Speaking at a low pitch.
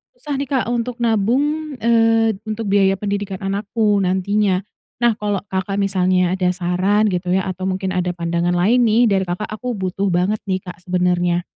No: high, 195 Hz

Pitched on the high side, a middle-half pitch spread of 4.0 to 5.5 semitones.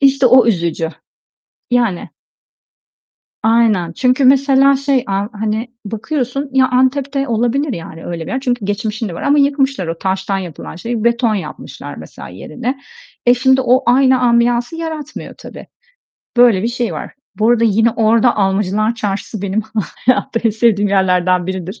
Yes: high, 230 Hz; average, 4.6 semitones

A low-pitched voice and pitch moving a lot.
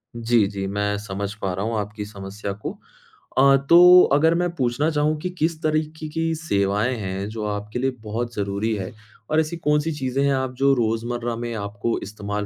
Yes: low, 120 Hz; wide, 6.5 semitones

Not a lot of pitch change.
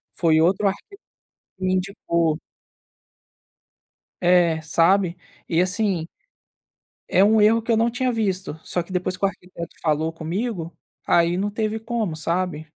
No: average, 3.8 semitones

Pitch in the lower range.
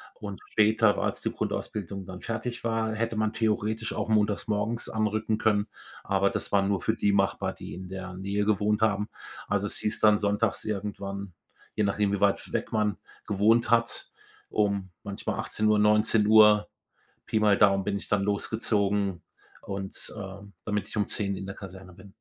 Yes: low, 105 Hz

